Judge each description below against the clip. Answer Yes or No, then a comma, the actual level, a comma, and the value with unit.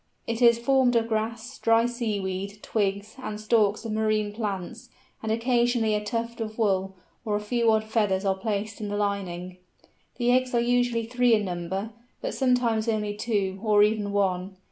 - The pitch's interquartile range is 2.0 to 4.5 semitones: Yes, narrow, 2.6 semitones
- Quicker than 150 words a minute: Yes, average, 180 wpm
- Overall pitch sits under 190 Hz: No, high, 215 Hz